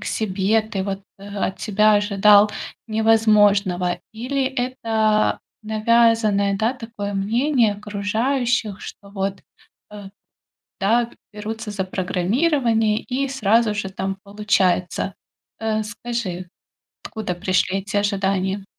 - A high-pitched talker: Yes, high, 210 Hz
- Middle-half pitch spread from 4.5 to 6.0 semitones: No, narrow, 2.4 semitones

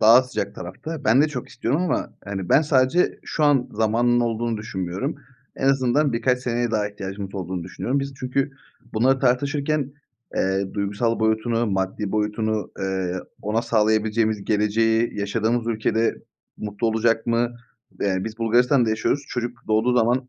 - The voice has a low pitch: Yes, low, 115 Hz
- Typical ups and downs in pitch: Yes, average, 3.2 semitones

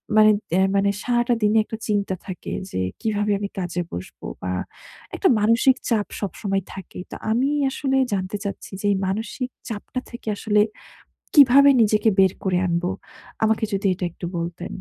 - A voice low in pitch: No, high, 205 Hz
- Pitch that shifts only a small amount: No, average, 3.3 semitones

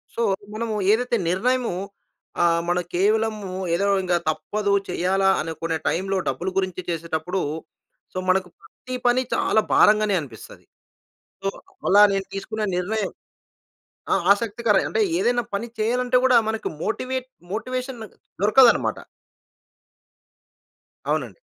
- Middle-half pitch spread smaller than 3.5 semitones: No, average, 4.3 semitones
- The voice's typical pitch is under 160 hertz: No, high, 210 Hz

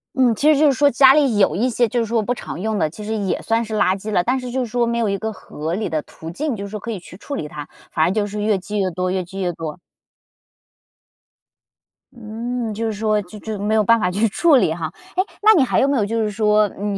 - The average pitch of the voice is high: Yes, high, 215 Hz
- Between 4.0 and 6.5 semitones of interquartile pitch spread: No, average, 3.6 semitones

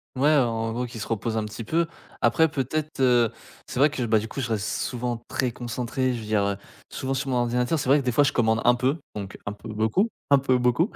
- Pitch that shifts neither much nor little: Yes, average, 3.1 semitones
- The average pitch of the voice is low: Yes, low, 125 Hz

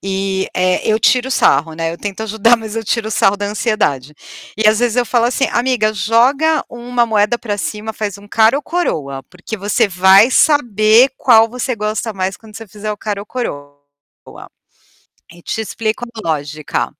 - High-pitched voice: Yes, high, 215 Hz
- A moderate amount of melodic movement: Yes, average, 3.4 semitones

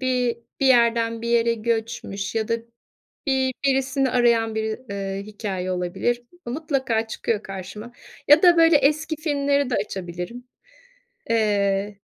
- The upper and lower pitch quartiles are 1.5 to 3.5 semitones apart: No, average, 4.2 semitones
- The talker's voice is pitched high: Yes, high, 230 Hz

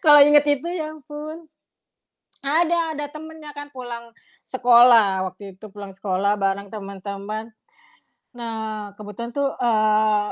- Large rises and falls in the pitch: Yes, wide, 6.1 semitones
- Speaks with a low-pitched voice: No, high, 235 Hz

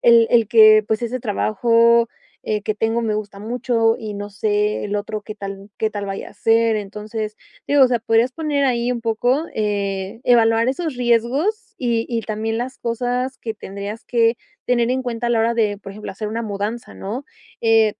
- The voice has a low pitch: No, high, 225 Hz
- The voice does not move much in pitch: Yes, narrow, 2.1 semitones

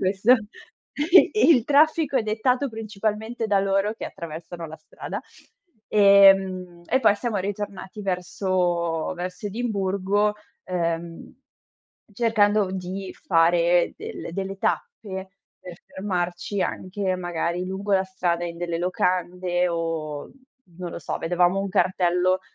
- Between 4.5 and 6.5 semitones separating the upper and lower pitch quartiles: No, average, 2.8 semitones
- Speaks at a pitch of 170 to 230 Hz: Yes, high, 190 Hz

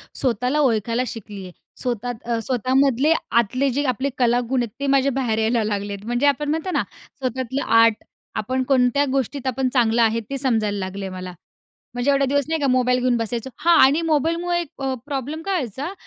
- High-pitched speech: Yes, very high, 255 Hz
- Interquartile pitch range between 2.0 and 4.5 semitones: Yes, average, 3.5 semitones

